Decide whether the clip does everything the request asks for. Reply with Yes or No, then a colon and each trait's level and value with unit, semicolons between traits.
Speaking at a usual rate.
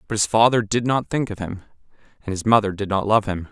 No: fast, 255 wpm